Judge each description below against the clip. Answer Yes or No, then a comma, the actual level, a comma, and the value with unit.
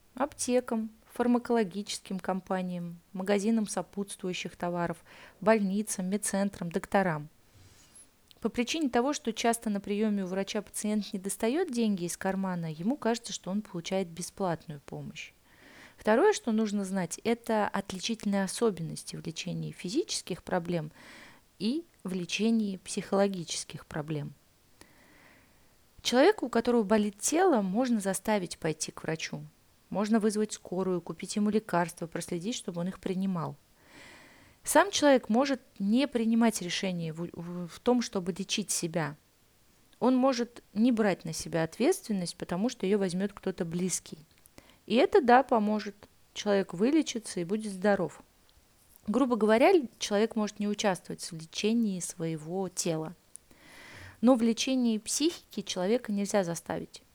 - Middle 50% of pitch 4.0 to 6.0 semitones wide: Yes, average, 4.3 semitones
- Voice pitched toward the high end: Yes, high, 200 Hz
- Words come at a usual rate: Yes, average, 125 wpm